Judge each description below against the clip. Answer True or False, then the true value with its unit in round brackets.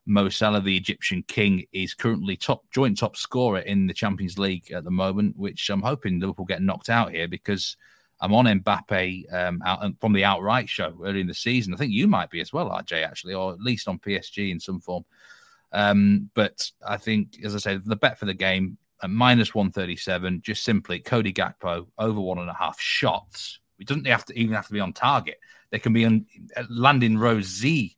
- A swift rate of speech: True (215 wpm)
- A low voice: True (100 Hz)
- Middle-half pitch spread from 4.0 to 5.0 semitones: False (2.5 semitones)